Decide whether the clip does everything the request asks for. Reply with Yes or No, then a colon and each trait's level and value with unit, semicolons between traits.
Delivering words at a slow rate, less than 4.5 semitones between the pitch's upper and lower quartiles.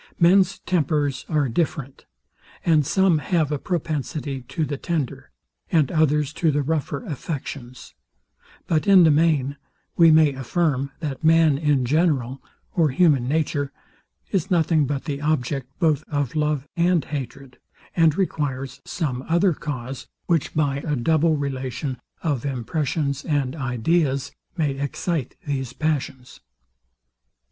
Yes: slow, 130 wpm; average, 3.0 semitones